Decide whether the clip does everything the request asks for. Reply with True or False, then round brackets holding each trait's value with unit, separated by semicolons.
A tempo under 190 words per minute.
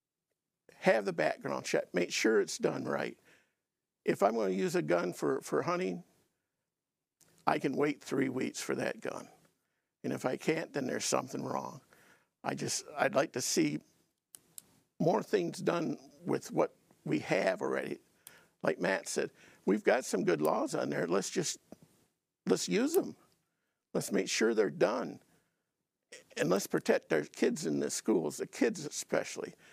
True (165 wpm)